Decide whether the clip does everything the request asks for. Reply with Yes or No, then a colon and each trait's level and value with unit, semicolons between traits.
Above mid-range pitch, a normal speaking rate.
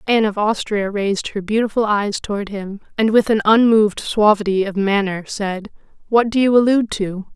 Yes: high, 210 Hz; average, 180 wpm